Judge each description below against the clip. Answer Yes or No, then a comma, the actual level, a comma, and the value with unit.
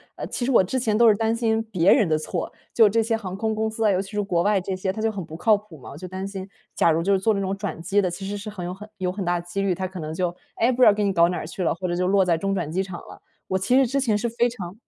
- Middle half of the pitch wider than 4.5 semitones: No, average, 3.3 semitones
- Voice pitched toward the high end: Yes, high, 195 Hz